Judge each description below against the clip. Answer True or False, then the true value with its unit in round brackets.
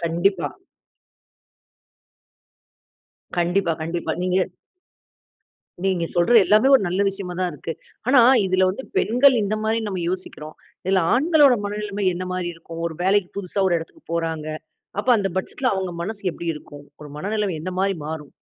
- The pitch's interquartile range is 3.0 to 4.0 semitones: True (3.4 semitones)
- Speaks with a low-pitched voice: False (185 Hz)